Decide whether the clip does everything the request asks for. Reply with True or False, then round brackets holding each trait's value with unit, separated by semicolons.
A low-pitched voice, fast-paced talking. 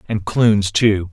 False (105 Hz; 160 wpm)